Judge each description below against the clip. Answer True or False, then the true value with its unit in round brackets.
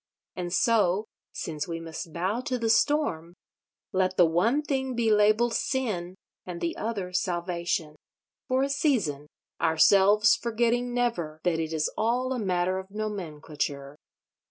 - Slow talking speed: True (130 wpm)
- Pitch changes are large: True (5.7 semitones)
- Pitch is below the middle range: False (190 Hz)